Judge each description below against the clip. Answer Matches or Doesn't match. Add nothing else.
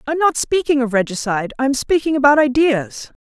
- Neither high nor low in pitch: Doesn't match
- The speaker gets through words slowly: Doesn't match